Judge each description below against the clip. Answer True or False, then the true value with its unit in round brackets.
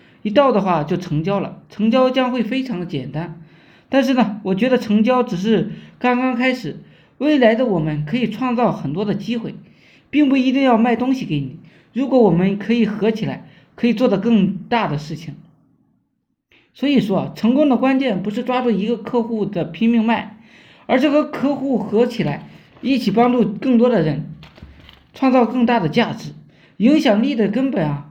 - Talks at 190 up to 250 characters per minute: False (265 characters per minute)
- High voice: True (230 Hz)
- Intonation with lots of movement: False (4.9 semitones)